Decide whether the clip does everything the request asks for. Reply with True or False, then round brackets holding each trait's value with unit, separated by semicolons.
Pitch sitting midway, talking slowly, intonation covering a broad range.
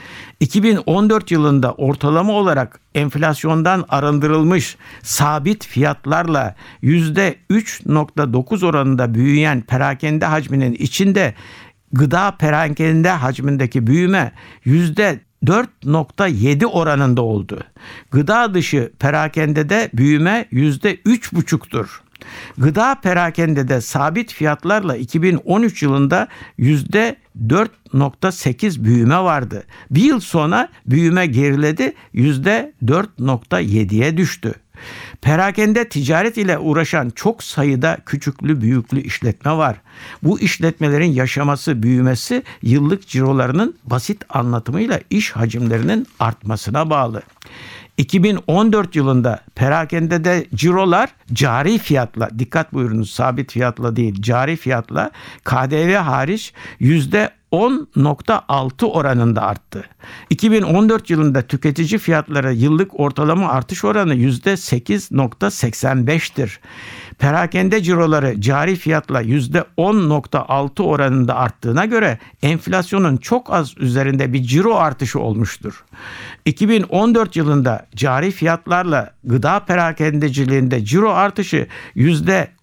True (150 Hz; 85 wpm; 5.7 semitones)